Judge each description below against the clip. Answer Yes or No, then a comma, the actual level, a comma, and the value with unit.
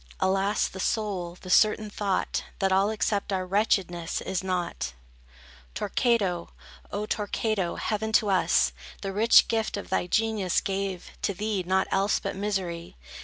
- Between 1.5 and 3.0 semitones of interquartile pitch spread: Yes, narrow, 2.4 semitones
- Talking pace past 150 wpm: No, average, 145 wpm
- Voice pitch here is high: Yes, high, 195 Hz